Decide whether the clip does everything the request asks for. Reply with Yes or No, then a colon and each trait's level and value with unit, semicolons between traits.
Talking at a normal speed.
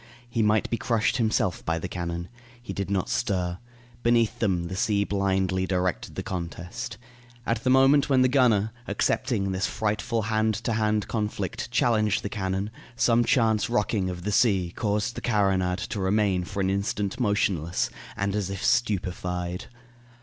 Yes: average, 165 wpm